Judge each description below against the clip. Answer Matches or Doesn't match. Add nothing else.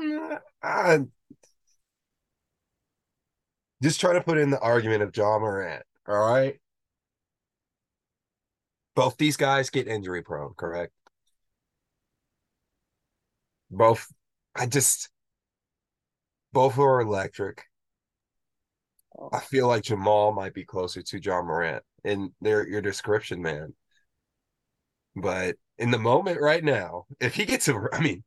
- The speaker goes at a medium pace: Doesn't match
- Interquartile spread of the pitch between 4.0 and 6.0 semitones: Matches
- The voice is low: Matches